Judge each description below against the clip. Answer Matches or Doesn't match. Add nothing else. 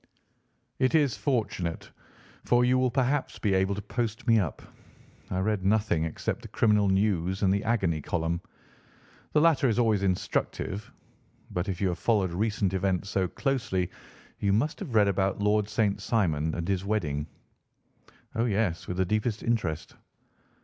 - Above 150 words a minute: Matches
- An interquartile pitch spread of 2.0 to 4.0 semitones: Matches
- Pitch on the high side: Doesn't match